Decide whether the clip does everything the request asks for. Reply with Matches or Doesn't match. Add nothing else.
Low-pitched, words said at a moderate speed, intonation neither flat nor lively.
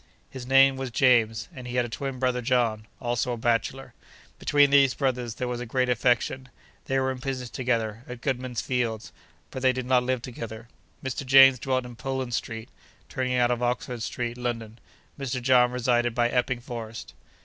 Doesn't match